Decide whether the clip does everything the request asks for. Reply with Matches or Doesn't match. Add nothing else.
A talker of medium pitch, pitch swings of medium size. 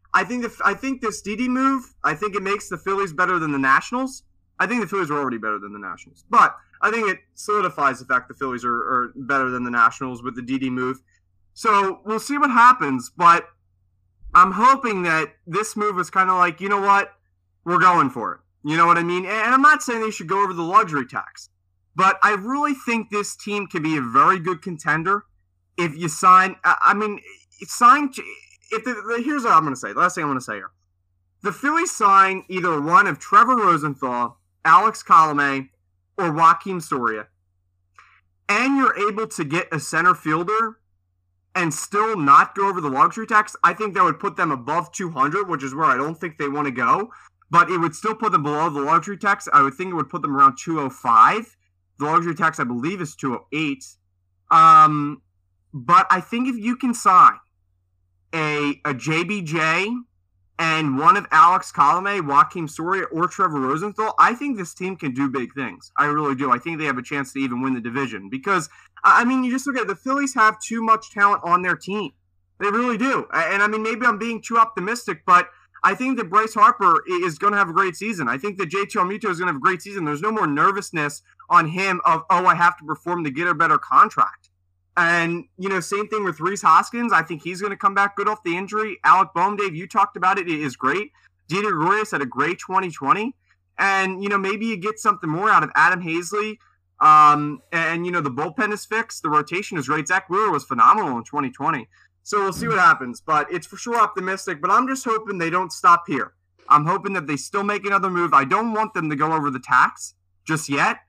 Doesn't match